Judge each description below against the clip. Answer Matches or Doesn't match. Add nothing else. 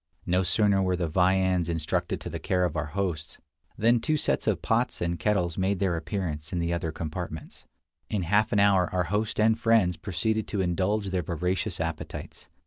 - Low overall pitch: Matches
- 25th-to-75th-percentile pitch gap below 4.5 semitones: Matches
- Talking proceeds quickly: Doesn't match